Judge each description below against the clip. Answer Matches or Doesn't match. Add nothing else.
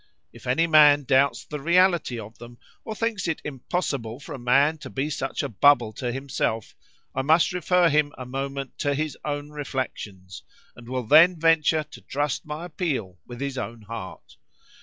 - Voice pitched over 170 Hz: Doesn't match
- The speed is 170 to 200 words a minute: Matches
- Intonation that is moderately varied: Matches